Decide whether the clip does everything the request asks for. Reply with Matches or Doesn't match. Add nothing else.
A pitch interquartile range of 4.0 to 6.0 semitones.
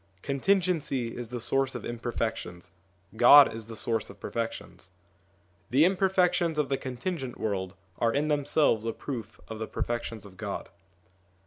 Matches